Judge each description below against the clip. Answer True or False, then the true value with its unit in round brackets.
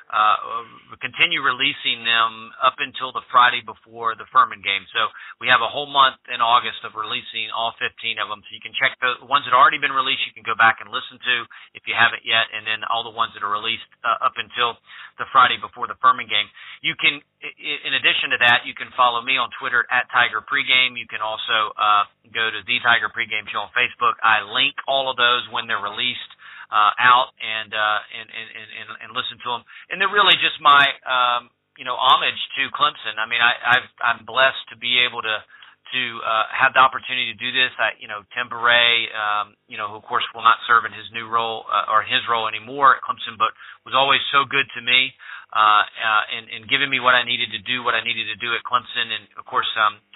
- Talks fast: True (230 wpm)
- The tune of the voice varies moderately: False (2.1 semitones)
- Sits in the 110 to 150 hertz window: True (120 Hz)